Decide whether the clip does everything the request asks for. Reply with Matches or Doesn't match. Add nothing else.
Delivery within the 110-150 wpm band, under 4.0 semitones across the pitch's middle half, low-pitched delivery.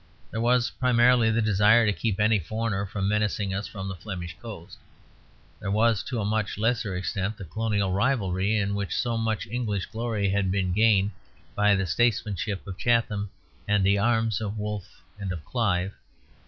Doesn't match